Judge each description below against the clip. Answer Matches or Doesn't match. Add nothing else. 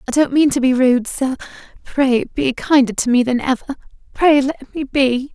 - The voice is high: Matches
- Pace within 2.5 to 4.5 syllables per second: Doesn't match